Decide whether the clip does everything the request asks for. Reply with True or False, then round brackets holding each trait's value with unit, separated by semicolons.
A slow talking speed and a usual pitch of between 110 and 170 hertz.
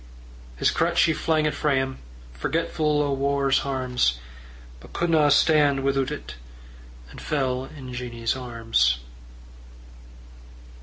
True (115 wpm; 135 Hz)